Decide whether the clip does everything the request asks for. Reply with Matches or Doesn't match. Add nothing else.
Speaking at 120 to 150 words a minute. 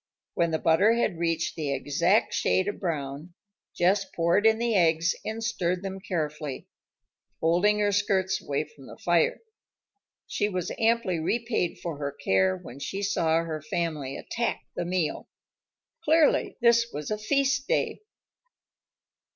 Matches